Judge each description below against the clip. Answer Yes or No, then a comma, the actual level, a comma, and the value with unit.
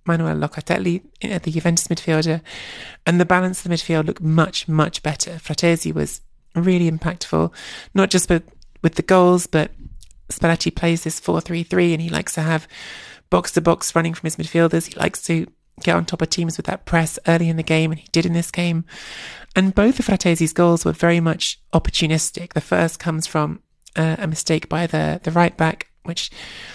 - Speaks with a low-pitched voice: No, medium, 165 Hz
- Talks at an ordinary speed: Yes, average, 195 wpm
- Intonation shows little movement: Yes, narrow, 1.4 semitones